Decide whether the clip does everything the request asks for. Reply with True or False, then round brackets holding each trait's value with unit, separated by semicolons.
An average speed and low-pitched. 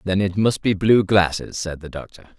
False (225 wpm; 95 Hz)